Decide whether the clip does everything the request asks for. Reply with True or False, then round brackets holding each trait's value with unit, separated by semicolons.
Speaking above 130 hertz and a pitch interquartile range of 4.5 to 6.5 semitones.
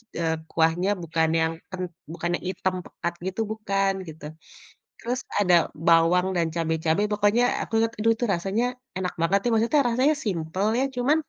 True (190 Hz; 5.1 semitones)